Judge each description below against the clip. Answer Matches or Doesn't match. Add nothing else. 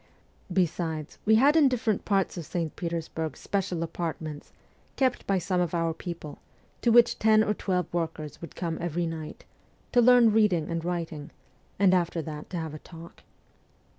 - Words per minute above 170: Doesn't match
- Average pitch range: Matches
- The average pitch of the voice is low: Doesn't match